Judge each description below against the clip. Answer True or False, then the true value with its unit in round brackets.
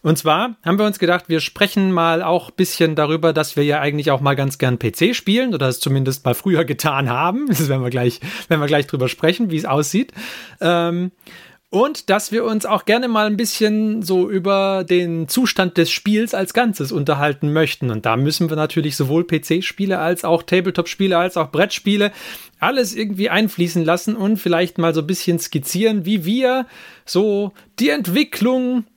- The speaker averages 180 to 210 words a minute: True (185 wpm)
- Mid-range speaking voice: True (175 Hz)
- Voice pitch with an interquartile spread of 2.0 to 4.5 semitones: False (5.1 semitones)